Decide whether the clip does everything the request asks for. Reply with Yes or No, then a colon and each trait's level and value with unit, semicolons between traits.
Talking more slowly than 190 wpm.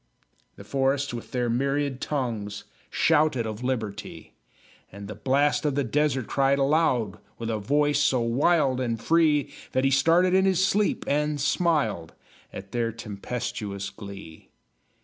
Yes: average, 145 wpm